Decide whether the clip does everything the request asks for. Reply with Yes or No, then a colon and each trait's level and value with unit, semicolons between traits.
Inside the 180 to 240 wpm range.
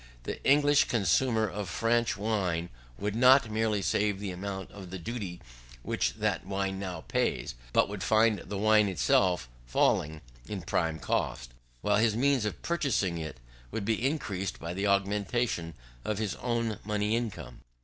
No: average, 160 wpm